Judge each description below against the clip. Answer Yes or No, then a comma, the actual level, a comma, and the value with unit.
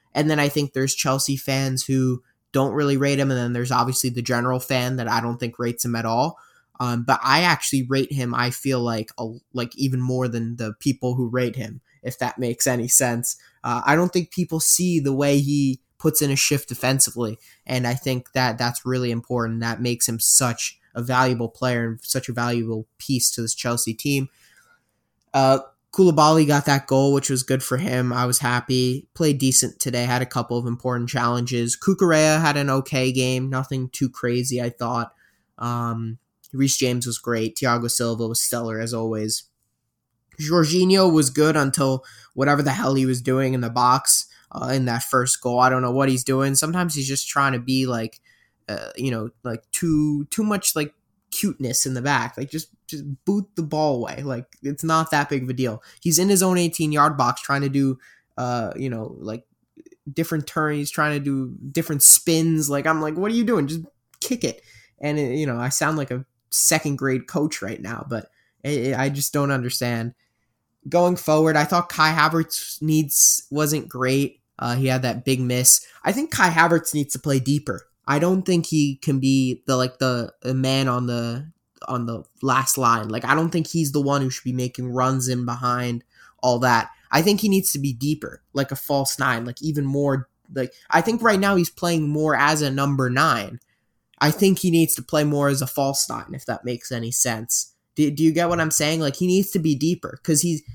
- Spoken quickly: Yes, fast, 210 wpm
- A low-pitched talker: Yes, low, 130 Hz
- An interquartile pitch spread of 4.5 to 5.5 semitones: No, average, 3.5 semitones